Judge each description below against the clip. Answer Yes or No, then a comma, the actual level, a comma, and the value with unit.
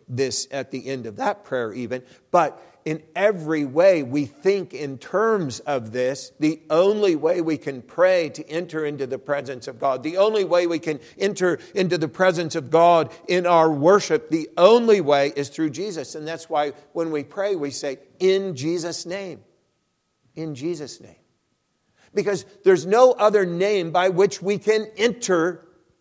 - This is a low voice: No, medium, 165 Hz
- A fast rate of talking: No, average, 175 wpm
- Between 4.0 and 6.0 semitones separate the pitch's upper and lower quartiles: Yes, average, 4.9 semitones